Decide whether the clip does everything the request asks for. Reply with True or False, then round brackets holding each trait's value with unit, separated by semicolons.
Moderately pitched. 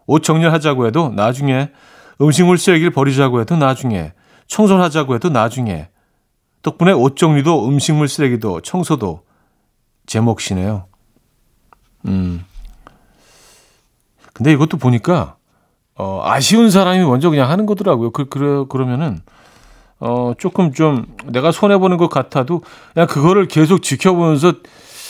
True (145 Hz)